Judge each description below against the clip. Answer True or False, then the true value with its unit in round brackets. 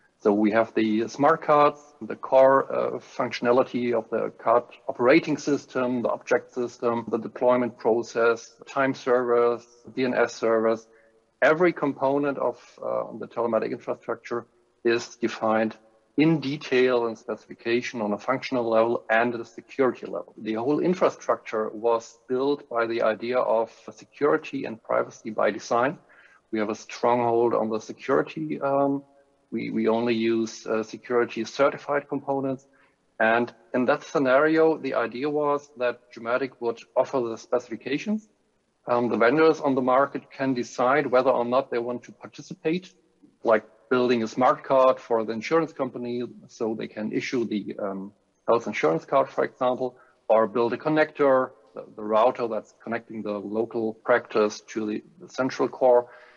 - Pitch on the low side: True (120 Hz)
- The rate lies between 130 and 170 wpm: True (150 wpm)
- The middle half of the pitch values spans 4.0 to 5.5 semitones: False (3.4 semitones)